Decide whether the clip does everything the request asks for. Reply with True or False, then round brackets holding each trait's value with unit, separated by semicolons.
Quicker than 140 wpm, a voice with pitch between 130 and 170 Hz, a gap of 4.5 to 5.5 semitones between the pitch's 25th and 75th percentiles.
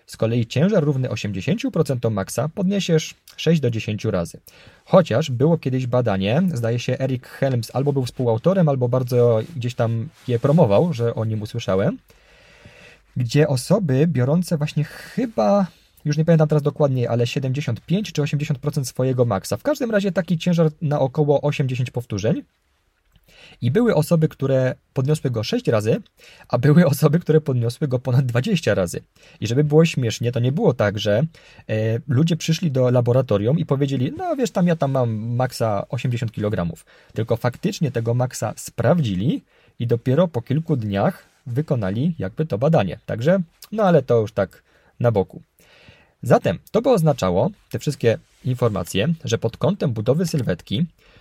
True (155 wpm; 135 Hz; 5.1 semitones)